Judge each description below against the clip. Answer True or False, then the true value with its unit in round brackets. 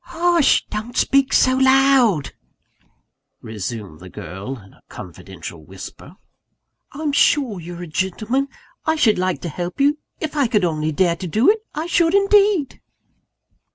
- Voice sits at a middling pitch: False (215 Hz)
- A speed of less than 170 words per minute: True (150 wpm)